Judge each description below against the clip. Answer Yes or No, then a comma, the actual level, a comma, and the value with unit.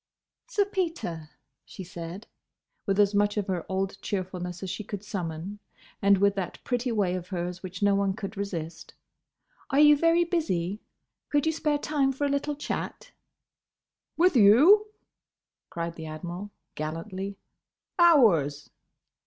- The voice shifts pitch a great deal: Yes, wide, 7.6 semitones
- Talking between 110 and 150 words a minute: Yes, average, 145 wpm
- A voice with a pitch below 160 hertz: No, high, 200 Hz